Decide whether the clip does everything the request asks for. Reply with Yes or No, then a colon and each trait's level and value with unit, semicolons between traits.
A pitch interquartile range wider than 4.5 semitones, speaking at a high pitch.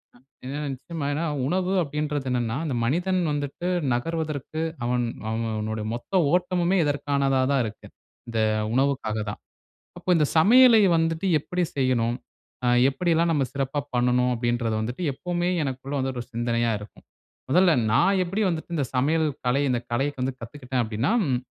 No: average, 5.2 semitones; medium, 140 Hz